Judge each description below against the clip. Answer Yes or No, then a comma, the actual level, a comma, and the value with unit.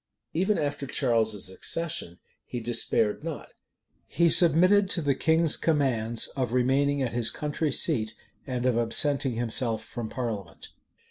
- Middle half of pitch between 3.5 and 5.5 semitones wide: Yes, average, 4.9 semitones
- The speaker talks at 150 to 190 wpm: No, slow, 135 wpm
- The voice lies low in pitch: Yes, low, 130 Hz